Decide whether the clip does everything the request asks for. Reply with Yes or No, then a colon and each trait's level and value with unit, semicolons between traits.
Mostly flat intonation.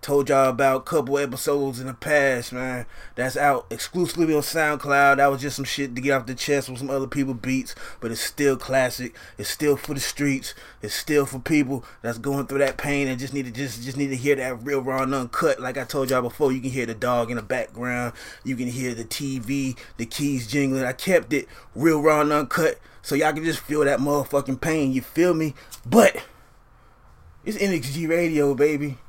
Yes: narrow, 2.0 semitones